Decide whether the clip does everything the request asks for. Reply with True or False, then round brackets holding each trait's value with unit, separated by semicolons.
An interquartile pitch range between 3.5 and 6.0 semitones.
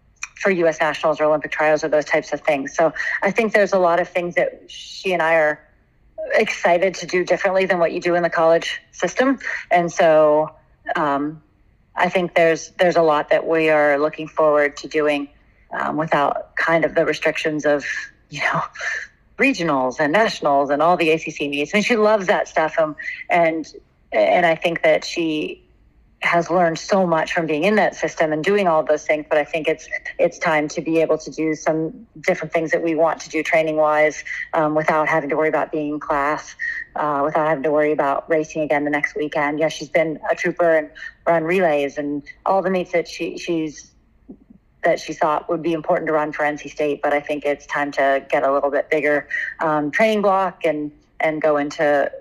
False (2.7 semitones)